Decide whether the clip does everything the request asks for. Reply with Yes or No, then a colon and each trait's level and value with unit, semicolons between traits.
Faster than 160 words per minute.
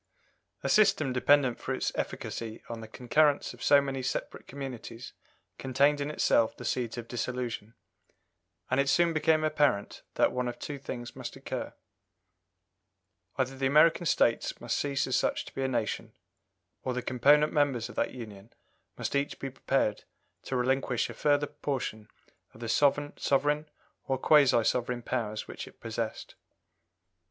No: average, 155 wpm